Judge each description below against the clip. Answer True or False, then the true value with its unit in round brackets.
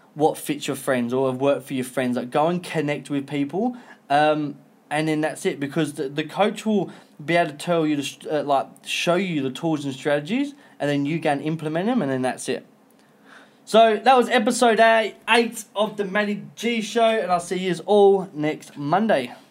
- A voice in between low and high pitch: True (165 Hz)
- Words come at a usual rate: False (210 wpm)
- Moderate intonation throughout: False (6.9 semitones)